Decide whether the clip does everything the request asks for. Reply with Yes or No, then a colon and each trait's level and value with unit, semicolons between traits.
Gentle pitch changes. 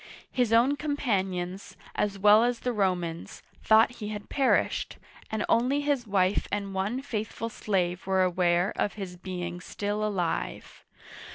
No: average, 3.8 semitones